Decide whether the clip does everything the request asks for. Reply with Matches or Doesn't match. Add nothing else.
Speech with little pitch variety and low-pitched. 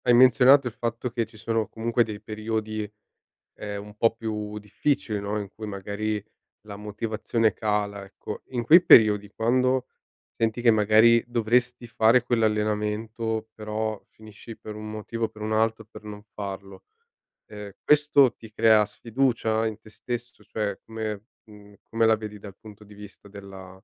Matches